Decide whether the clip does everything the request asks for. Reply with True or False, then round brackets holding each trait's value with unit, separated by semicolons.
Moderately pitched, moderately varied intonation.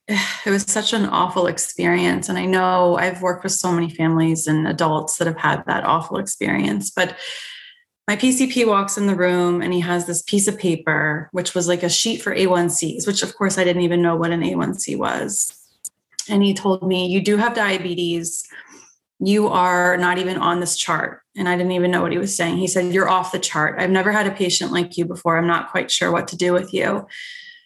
False (180 Hz; 2.3 semitones)